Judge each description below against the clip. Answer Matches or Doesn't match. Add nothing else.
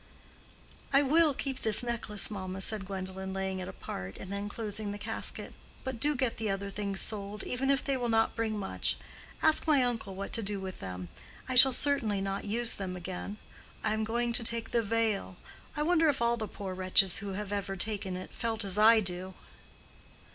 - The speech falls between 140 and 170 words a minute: Doesn't match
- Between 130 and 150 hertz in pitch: Doesn't match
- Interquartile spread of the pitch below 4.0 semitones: Matches